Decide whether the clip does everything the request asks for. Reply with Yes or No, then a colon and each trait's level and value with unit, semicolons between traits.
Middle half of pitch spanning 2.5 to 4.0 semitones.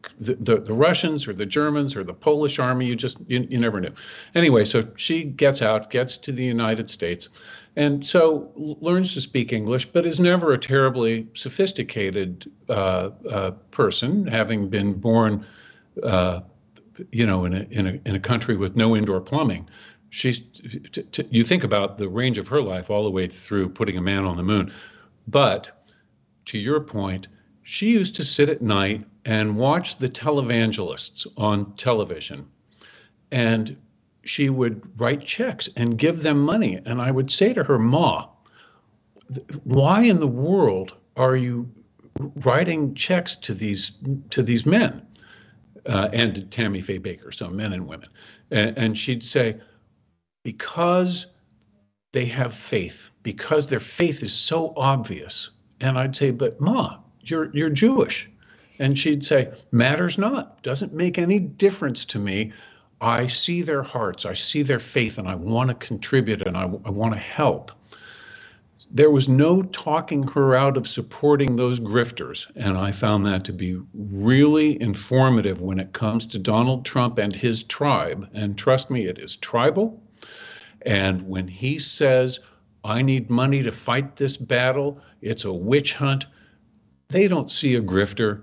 No: wide, 5.5 semitones